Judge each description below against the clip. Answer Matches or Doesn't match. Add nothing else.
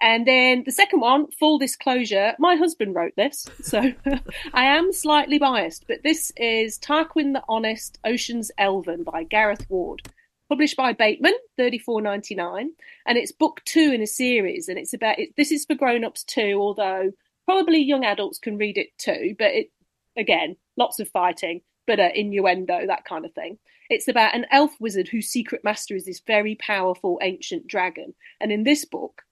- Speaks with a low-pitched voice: Doesn't match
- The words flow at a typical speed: Matches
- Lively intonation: Matches